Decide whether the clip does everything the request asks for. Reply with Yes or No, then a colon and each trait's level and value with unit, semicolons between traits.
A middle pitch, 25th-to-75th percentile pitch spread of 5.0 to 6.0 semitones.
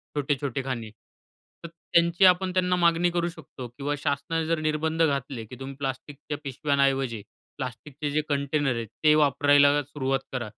No: medium, 145 Hz; average, 3.0 semitones